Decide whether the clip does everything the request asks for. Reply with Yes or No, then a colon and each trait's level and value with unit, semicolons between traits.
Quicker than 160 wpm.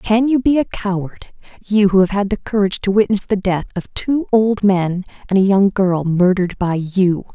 Yes: fast, 205 wpm